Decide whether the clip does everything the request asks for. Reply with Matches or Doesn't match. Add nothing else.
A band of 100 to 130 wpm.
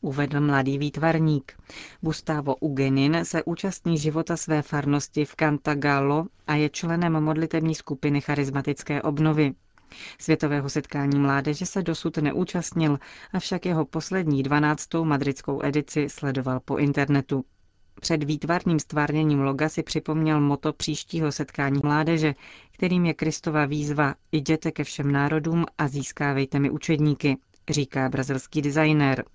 Matches